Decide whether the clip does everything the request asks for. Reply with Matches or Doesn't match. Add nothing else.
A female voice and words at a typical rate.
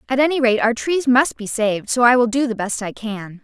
Doesn't match